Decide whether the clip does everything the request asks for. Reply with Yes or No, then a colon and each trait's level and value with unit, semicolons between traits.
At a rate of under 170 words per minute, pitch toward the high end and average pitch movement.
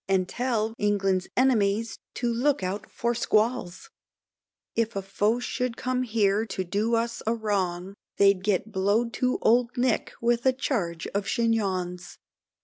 Yes: average, 140 wpm; high, 220 Hz; average, 3.4 semitones